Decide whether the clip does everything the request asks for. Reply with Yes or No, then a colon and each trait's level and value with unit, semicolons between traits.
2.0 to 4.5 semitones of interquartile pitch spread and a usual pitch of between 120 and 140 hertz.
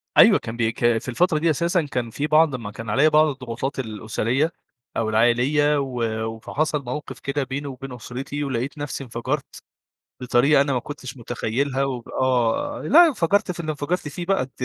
Yes: average, 3.7 semitones; low, 135 Hz